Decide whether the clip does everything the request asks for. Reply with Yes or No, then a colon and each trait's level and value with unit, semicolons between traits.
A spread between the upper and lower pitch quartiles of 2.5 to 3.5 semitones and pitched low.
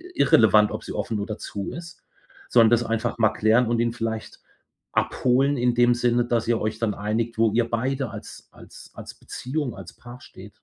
No: narrow, 1.8 semitones; low, 115 Hz